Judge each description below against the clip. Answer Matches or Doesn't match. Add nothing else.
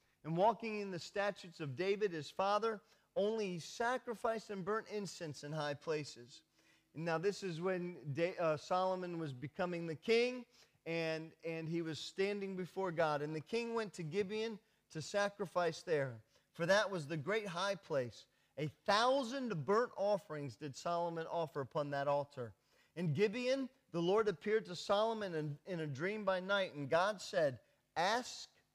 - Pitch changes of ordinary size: Matches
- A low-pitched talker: Doesn't match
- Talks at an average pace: Matches